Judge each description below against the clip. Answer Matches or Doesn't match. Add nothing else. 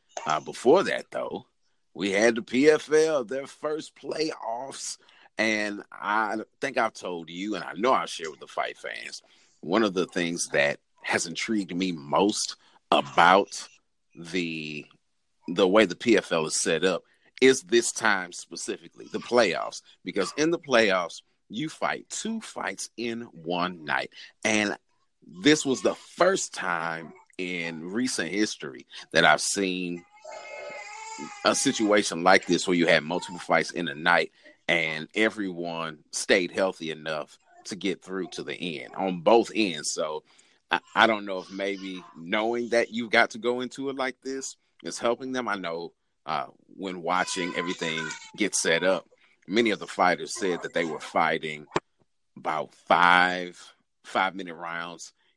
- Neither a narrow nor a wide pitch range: Doesn't match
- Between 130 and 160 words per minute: Matches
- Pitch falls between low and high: Doesn't match